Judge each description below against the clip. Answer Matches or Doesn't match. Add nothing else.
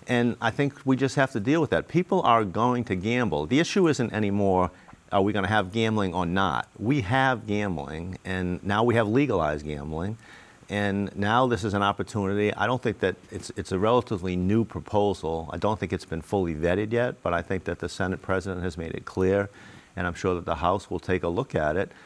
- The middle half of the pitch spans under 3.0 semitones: Doesn't match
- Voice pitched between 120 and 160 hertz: Doesn't match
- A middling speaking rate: Doesn't match